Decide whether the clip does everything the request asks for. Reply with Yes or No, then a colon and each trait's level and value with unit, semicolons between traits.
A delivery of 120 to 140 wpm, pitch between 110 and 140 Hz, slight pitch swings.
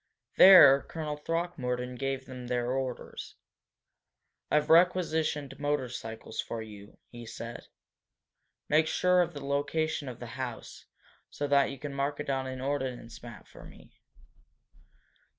No: slow, 135 wpm; low, 135 Hz; average, 3.2 semitones